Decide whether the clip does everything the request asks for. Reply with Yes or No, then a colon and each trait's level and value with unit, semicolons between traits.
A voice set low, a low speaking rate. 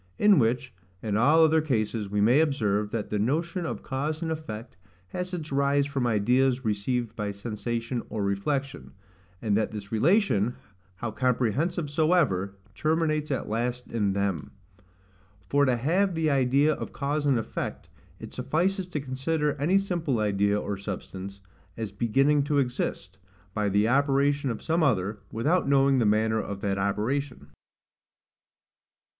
No: low, 125 Hz; average, 150 wpm